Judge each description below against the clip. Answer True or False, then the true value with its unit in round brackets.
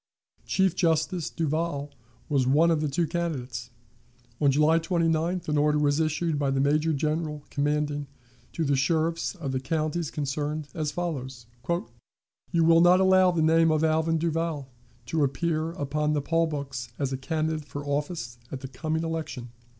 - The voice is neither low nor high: True (155 Hz)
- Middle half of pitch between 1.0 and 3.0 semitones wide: True (2.5 semitones)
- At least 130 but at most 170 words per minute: True (165 wpm)